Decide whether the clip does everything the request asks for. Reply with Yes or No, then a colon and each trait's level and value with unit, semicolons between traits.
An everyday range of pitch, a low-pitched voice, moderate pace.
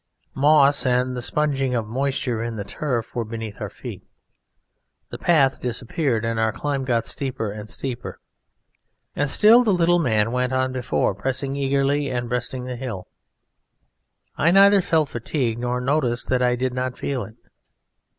Yes: average, 3.0 semitones; low, 125 Hz; average, 160 wpm